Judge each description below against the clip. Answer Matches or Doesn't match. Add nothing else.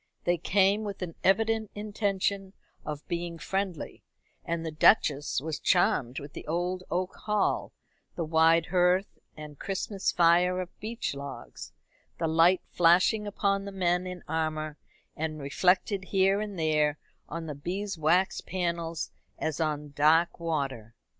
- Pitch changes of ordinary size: Matches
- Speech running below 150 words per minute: Matches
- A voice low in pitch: Doesn't match